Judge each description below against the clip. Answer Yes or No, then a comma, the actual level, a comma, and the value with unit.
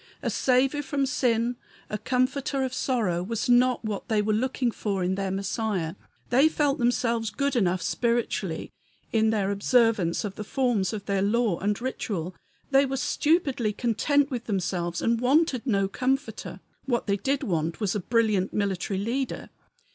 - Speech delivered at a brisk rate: No, average, 160 wpm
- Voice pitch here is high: Yes, high, 230 Hz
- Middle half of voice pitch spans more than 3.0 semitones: Yes, average, 4.4 semitones